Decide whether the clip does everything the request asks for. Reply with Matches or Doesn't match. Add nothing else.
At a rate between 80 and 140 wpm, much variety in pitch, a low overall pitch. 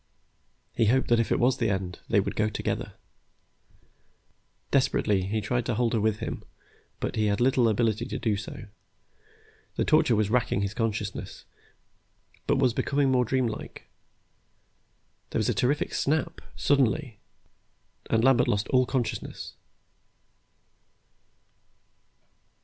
Doesn't match